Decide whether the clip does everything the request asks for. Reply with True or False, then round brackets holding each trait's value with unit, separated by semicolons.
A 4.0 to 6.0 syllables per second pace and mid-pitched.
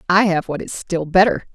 True (5.3 syllables/s; 180 Hz)